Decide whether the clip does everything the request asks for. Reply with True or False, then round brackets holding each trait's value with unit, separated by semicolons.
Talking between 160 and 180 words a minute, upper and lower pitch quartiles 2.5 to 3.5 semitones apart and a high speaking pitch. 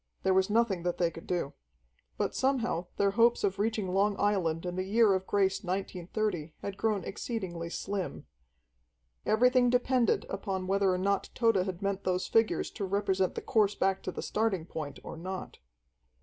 True (175 wpm; 2.8 semitones; 195 Hz)